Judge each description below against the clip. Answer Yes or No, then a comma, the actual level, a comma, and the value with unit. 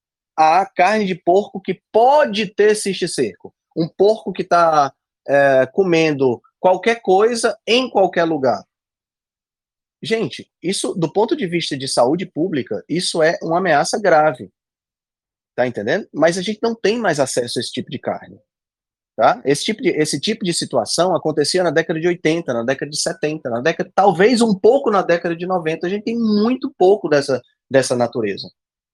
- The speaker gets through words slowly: No, average, 170 wpm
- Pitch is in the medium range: Yes, medium, 175 Hz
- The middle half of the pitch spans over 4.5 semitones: Yes, average, 5.0 semitones